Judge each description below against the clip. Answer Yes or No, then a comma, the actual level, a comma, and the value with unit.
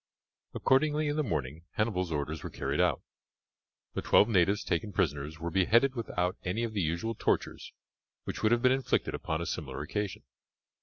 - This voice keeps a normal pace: Yes, average, 170 wpm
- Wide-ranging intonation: Yes, wide, 6.3 semitones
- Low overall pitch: Yes, very low, 95 Hz